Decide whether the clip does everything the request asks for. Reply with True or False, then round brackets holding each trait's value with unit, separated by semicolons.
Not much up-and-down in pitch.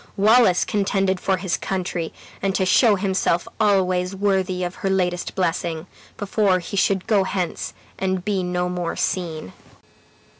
True (1.6 semitones)